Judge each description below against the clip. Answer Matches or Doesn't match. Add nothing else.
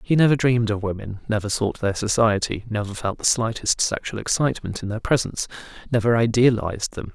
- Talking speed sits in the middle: Matches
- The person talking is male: Matches